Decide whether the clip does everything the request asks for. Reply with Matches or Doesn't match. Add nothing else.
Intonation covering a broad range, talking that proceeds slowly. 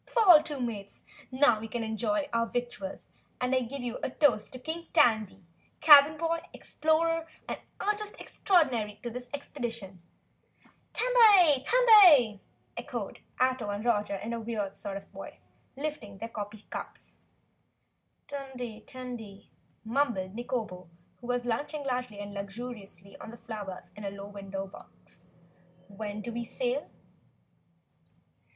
Matches